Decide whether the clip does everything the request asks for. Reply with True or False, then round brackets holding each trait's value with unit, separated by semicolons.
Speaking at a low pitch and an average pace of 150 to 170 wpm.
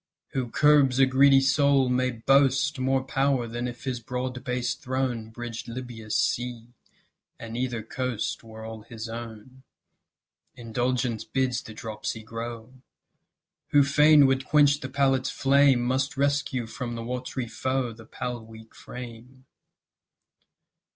False (125 Hz; 135 wpm)